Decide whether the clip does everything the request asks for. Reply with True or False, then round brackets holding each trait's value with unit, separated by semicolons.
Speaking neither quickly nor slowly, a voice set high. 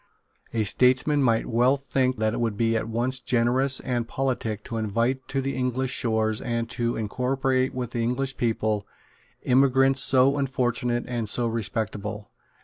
False (155 wpm; 120 Hz)